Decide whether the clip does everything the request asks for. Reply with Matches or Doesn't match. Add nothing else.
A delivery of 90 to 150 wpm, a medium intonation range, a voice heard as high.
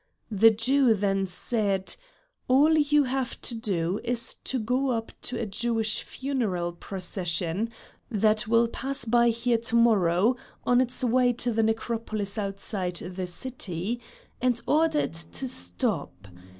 Matches